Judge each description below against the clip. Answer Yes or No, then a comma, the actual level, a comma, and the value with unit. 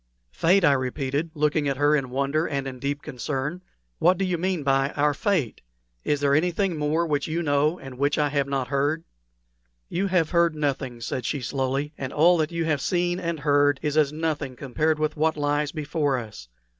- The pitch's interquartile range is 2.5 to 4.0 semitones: Yes, average, 2.8 semitones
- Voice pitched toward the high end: No, medium, 150 Hz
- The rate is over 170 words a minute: Yes, average, 200 wpm